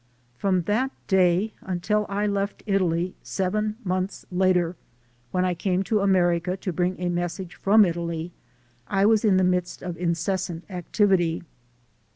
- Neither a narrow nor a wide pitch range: No, narrow, 2.1 semitones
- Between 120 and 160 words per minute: Yes, average, 145 wpm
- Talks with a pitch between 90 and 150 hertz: No, medium, 185 Hz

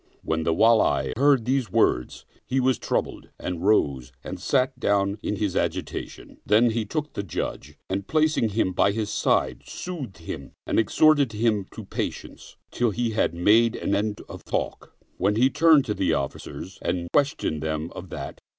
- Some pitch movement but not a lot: No, wide, 5.8 semitones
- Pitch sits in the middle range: No, low, 105 Hz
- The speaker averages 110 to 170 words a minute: No, average, 180 wpm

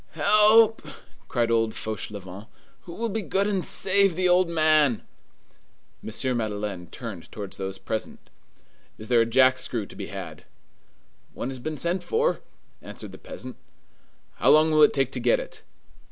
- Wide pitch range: Yes, wide, 8.7 semitones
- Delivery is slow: No, average, 160 wpm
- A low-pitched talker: Yes, low, 130 Hz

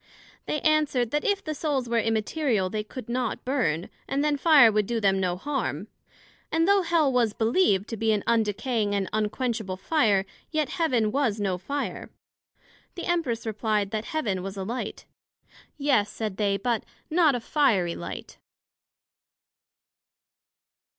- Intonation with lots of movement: Yes, wide, 5.8 semitones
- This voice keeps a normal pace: Yes, average, 150 wpm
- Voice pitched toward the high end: Yes, high, 230 Hz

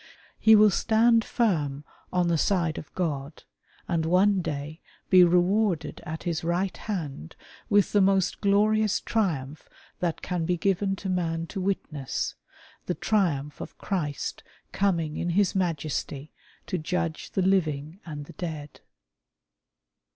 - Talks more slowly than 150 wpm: Yes, average, 140 wpm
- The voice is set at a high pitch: No, medium, 175 Hz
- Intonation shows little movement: No, average, 4.0 semitones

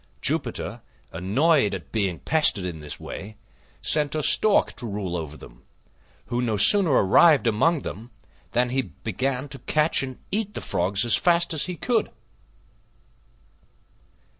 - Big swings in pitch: Yes, wide, 7.8 semitones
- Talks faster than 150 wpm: No, average, 145 wpm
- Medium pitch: No, low, 125 Hz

